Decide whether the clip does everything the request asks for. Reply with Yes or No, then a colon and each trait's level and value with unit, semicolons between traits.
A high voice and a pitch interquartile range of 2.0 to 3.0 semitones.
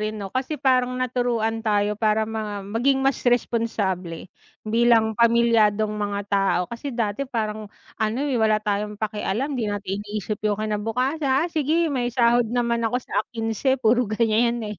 Yes: high, 225 Hz; narrow, 2.5 semitones